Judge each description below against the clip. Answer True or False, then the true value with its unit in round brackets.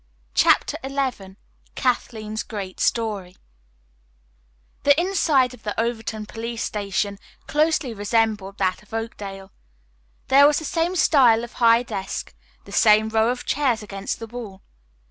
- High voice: True (225 Hz)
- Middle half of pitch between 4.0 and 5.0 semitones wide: False (3.6 semitones)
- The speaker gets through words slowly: True (130 wpm)